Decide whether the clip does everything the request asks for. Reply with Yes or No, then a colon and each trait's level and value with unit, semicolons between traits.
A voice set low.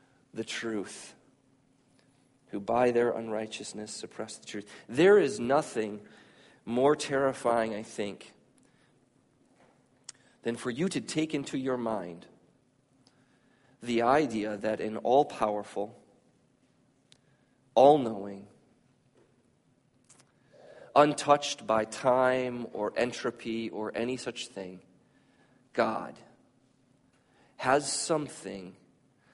Yes: low, 120 Hz